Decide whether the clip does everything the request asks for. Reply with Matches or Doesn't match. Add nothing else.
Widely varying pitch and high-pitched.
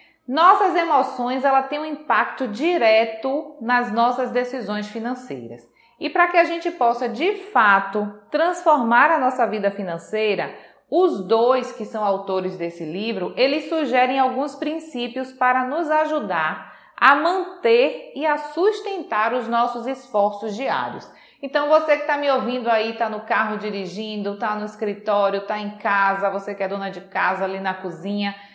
Matches